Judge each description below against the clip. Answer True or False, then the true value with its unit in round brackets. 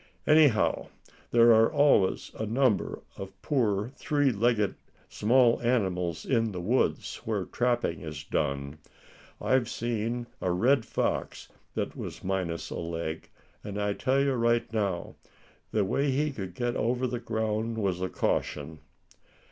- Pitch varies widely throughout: False (4.6 semitones)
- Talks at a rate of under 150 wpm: True (140 wpm)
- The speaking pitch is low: True (110 Hz)